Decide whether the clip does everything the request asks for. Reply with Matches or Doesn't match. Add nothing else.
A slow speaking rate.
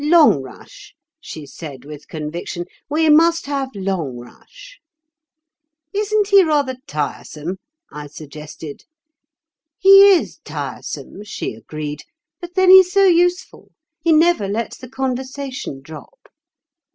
Matches